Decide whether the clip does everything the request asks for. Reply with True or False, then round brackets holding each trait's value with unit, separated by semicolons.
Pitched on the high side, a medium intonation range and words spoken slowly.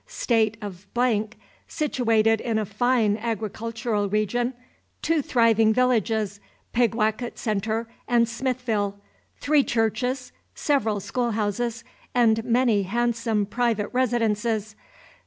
False (225 Hz; 2.2 semitones; 100 wpm)